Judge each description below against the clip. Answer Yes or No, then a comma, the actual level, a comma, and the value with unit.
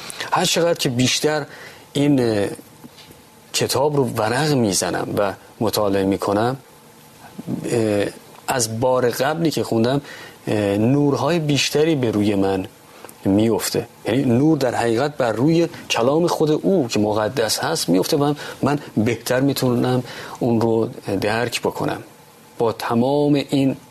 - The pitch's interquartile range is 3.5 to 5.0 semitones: Yes, average, 4.5 semitones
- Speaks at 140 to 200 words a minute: No, average, 120 wpm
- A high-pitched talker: No, low, 125 Hz